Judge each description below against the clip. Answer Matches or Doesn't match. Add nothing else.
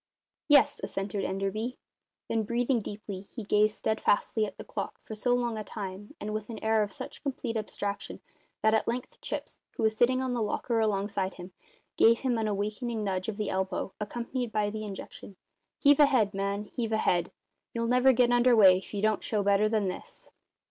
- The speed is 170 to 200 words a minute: Matches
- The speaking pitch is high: Matches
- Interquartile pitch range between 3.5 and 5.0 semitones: Doesn't match